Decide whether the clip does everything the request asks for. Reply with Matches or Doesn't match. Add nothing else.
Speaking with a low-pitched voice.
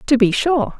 Doesn't match